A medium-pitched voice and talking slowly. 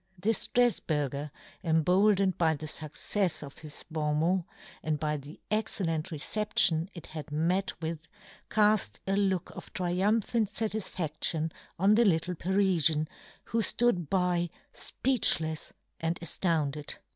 Yes: medium, 175 Hz; slow, 120 wpm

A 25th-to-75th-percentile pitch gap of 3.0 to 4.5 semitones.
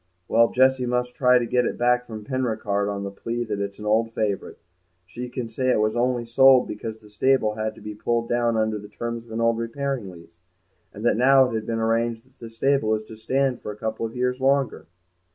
No: narrow, 2.5 semitones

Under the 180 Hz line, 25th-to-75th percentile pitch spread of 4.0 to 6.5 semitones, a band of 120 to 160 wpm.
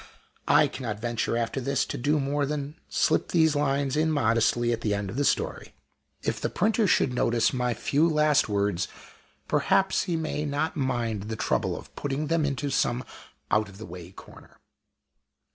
No: low, 135 Hz; average, 4.5 semitones; average, 180 wpm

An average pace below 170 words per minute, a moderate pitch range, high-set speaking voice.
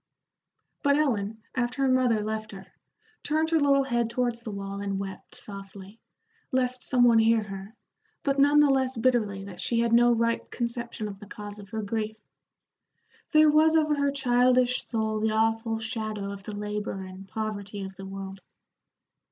No: average, 175 wpm; average, 3.8 semitones; high, 225 Hz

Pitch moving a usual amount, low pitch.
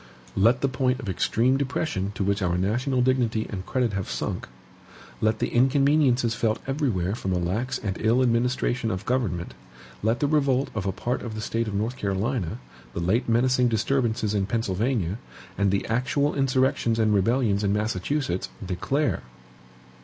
Yes: average, 4.4 semitones; low, 115 Hz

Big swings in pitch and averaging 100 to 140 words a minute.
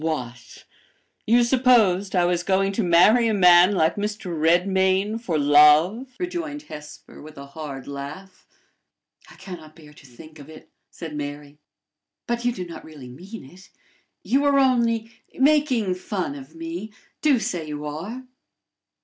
No: wide, 6.8 semitones; average, 155 wpm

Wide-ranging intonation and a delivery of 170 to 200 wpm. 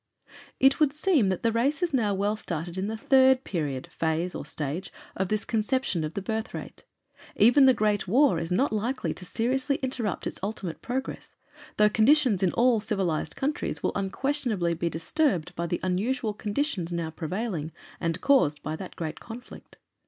Yes: wide, 6.9 semitones; average, 175 wpm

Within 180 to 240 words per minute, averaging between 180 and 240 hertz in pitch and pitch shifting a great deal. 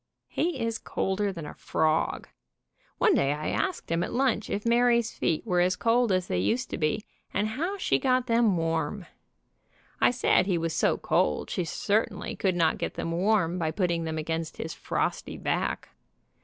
Yes: average, 185 wpm; medium, 185 Hz; wide, 5.9 semitones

